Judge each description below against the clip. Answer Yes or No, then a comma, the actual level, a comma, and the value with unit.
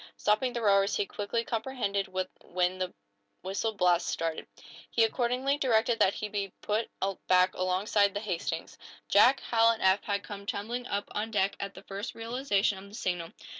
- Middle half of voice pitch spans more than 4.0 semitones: No, average, 3.1 semitones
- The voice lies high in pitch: Yes, high, 205 Hz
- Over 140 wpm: Yes, average, 170 wpm